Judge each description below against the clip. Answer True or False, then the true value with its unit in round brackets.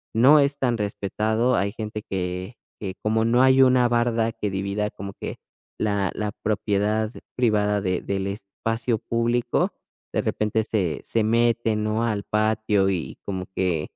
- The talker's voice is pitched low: True (110 Hz)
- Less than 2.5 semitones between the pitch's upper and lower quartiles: False (2.8 semitones)